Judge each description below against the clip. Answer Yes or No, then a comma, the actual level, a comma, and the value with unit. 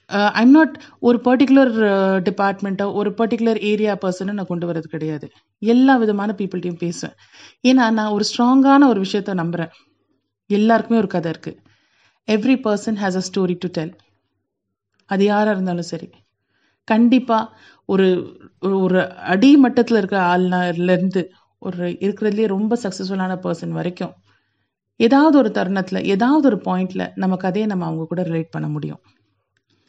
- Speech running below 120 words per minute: No, fast, 130 wpm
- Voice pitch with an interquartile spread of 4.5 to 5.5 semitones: No, average, 4.0 semitones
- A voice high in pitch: Yes, high, 195 Hz